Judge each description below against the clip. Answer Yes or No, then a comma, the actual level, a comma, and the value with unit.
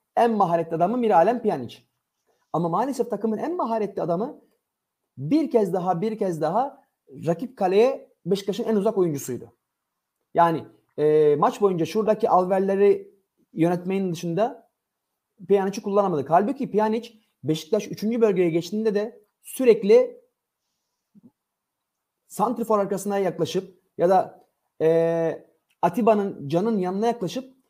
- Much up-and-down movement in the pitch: No, average, 4.8 semitones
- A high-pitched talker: Yes, high, 200 Hz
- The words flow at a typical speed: Yes, average, 110 wpm